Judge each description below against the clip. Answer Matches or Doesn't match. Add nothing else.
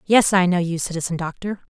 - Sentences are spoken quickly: Matches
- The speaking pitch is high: Doesn't match